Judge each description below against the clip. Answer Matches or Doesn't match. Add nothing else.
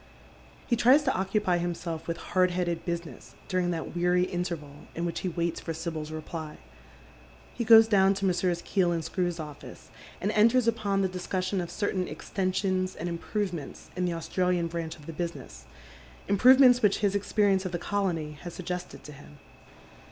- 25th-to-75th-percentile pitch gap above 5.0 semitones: Doesn't match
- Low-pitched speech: Doesn't match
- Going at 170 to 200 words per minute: Matches